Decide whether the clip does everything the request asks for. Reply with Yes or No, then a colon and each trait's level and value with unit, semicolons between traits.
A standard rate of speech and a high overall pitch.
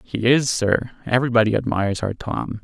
No: average, 160 wpm; low, 115 Hz